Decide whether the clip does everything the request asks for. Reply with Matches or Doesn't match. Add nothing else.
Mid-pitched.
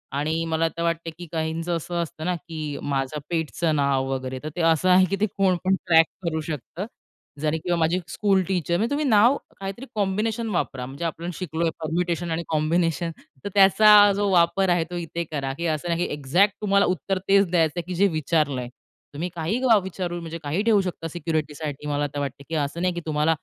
Matches